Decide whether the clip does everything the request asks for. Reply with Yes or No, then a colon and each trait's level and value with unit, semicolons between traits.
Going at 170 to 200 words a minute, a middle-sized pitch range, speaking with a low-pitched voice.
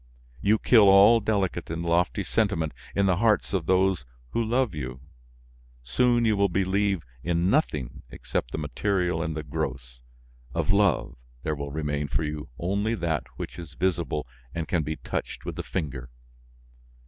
No: average, 160 wpm; average, 4.8 semitones; very low, 85 Hz